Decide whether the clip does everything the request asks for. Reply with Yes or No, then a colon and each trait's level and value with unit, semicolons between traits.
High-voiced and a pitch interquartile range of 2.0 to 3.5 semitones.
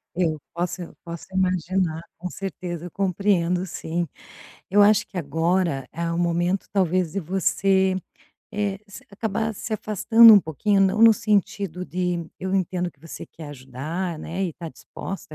No: medium, 180 Hz; narrow, 2.6 semitones